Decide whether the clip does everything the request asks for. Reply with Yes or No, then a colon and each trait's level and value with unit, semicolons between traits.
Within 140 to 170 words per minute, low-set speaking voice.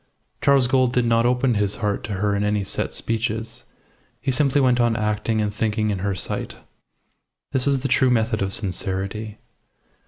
No: average, 180 wpm; low, 110 Hz